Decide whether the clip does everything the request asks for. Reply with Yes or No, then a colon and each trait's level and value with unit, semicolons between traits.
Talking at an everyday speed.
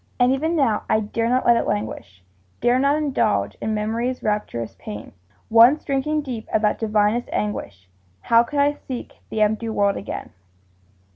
Yes: average, 165 wpm